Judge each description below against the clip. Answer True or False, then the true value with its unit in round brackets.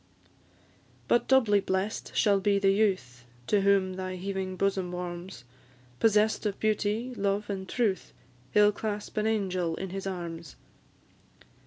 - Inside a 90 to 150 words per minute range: True (140 wpm)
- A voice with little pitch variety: True (2.0 semitones)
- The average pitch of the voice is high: True (195 Hz)